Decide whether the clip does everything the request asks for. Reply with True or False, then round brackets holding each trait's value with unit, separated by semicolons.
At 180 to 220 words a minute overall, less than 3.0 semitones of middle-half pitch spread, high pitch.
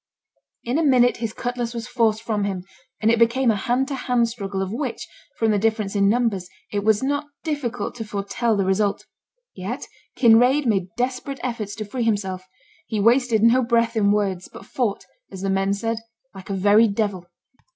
False (190 wpm; 3.3 semitones; 225 Hz)